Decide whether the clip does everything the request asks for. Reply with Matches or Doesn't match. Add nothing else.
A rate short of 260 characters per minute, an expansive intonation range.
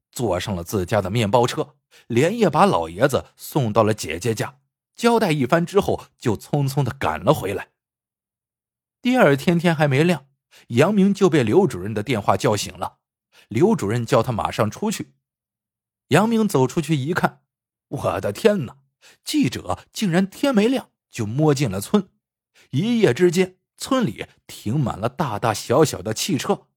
Matches